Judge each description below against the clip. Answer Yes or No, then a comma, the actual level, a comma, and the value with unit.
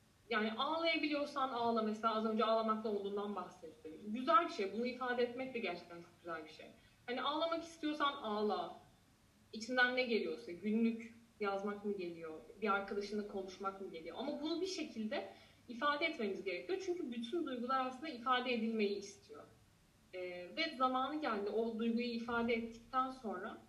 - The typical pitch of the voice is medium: No, high, 230 Hz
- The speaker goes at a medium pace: No, fast, 150 wpm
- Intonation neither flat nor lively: Yes, average, 4.6 semitones